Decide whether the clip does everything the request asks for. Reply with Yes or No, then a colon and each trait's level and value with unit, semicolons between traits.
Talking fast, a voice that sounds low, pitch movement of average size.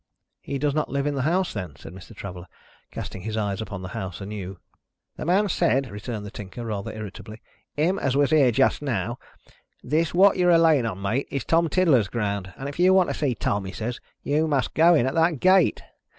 No: fast, 220 wpm; low, 130 Hz; wide, 7.6 semitones